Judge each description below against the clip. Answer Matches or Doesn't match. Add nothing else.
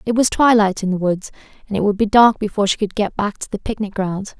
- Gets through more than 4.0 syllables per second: Matches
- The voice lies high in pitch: Matches